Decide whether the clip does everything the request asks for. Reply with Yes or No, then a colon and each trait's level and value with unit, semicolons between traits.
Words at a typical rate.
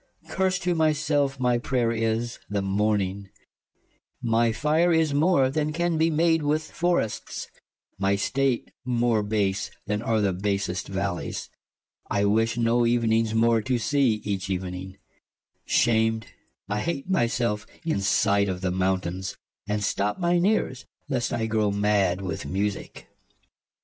Yes: average, 145 wpm